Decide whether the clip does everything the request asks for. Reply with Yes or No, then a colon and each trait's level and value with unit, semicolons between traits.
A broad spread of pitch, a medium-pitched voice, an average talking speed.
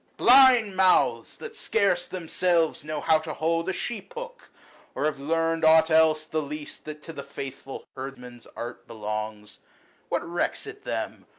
No: average, 4.7 semitones; medium, 160 Hz; average, 165 wpm